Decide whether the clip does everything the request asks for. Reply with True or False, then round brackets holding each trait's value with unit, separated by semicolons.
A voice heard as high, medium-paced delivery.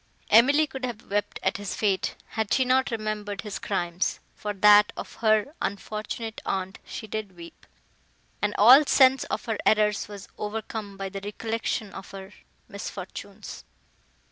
True (210 Hz; 150 wpm)